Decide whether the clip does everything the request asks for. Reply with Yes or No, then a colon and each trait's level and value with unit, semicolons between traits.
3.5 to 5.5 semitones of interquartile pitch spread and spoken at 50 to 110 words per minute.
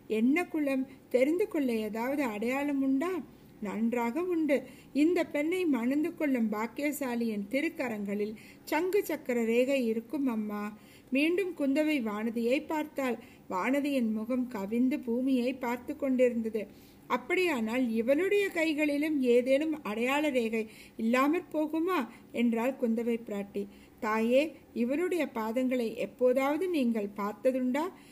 Yes: average, 4.4 semitones; average, 100 wpm